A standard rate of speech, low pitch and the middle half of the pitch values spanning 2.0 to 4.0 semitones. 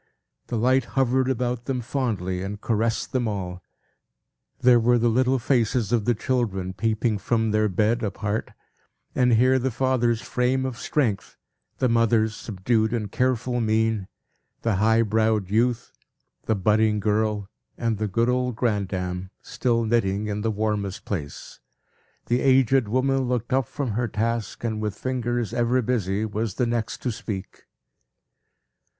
Yes: average, 150 wpm; low, 115 Hz; average, 2.7 semitones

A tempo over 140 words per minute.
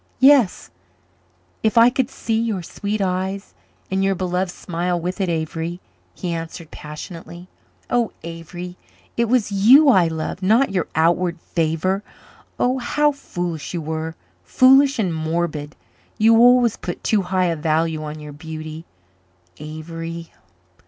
No: slow, 135 wpm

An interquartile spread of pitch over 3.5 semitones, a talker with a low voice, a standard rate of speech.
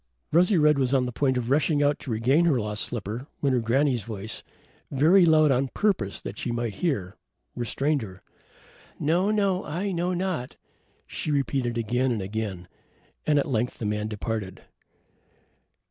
Yes: wide, 5.5 semitones; low, 130 Hz; average, 165 wpm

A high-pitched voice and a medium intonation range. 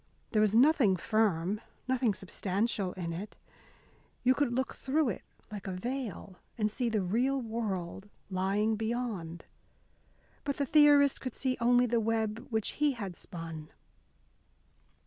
Yes: high, 220 Hz; average, 4.7 semitones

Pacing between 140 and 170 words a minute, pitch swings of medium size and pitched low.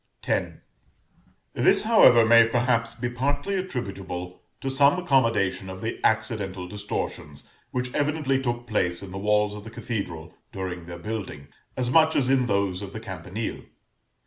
Yes: average, 150 wpm; average, 4.9 semitones; low, 110 Hz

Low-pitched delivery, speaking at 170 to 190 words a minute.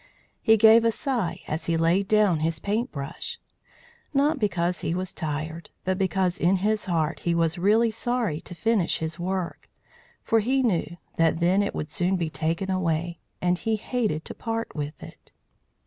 No: medium, 185 Hz; average, 175 wpm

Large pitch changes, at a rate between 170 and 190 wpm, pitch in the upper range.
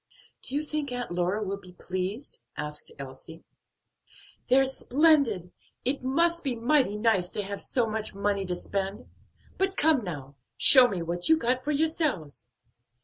No: wide, 7.4 semitones; average, 155 wpm; high, 220 Hz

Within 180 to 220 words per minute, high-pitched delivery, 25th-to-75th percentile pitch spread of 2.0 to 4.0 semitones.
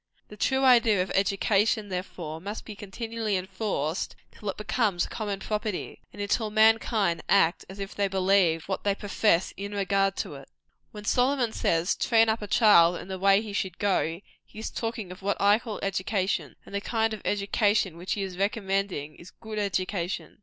Yes: average, 190 wpm; high, 200 Hz; narrow, 2.4 semitones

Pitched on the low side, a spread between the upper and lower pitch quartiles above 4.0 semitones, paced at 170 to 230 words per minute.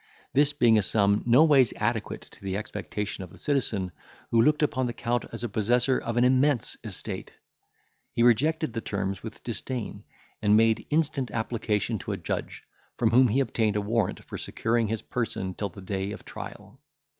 No: low, 115 Hz; average, 3.6 semitones; average, 180 wpm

